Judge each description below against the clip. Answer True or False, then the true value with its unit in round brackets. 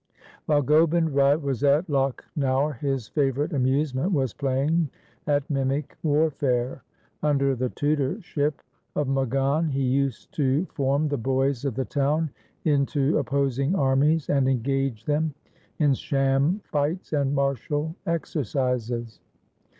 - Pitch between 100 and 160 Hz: True (140 Hz)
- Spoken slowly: True (120 wpm)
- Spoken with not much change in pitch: True (2.0 semitones)